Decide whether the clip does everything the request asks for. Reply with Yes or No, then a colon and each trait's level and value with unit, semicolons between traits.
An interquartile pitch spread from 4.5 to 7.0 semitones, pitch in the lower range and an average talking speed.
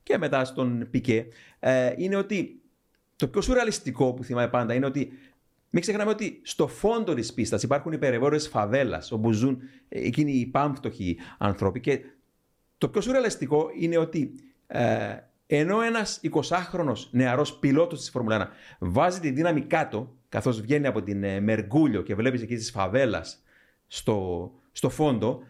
Yes: wide, 5.5 semitones; low, 130 Hz; average, 145 wpm